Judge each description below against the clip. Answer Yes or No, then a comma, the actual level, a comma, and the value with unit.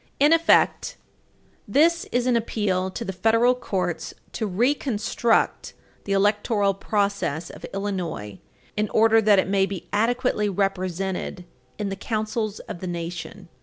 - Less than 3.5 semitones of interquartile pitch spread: Yes, average, 3.1 semitones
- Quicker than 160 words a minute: No, slow, 135 wpm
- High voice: Yes, high, 205 Hz